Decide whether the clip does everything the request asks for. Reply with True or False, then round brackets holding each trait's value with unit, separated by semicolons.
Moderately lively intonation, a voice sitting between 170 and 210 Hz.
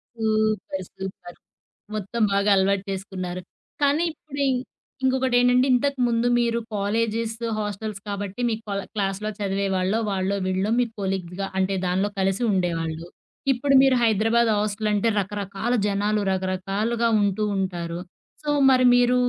True (3.4 semitones; 205 Hz)